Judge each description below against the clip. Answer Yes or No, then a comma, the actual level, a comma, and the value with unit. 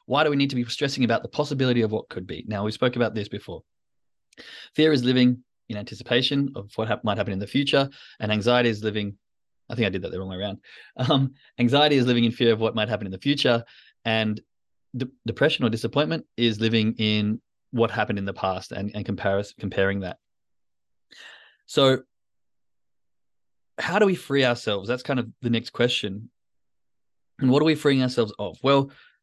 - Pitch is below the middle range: Yes, low, 120 Hz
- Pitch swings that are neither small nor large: Yes, average, 4.0 semitones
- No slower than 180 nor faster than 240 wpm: Yes, average, 200 wpm